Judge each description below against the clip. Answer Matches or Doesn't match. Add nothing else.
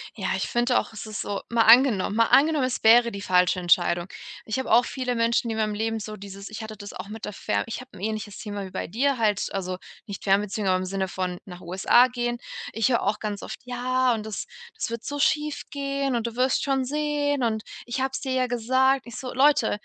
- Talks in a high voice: Matches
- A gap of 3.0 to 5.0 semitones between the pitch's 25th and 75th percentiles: Matches